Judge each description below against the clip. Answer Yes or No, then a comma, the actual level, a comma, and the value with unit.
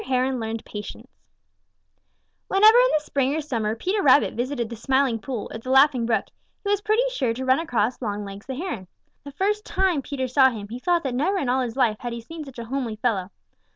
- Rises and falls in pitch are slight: No, average, 4.7 semitones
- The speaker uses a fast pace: Yes, fast, 220 wpm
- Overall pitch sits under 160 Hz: No, very high, 260 Hz